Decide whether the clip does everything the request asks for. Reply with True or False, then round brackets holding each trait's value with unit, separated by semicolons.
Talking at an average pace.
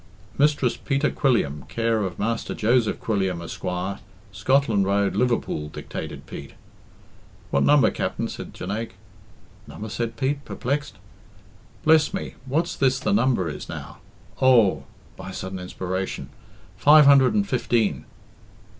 False (130 wpm)